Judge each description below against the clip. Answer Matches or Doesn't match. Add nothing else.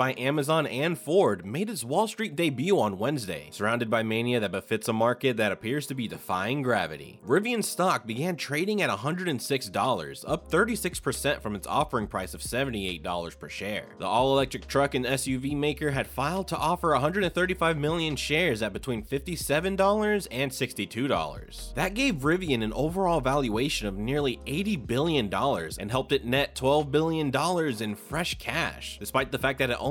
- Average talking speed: Matches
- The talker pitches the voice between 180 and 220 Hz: Doesn't match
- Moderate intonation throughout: Doesn't match